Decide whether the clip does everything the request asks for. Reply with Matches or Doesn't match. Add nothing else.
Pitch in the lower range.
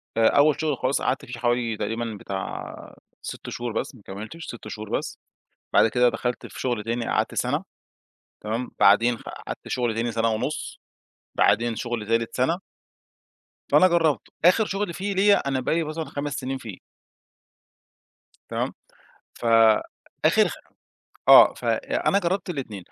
Matches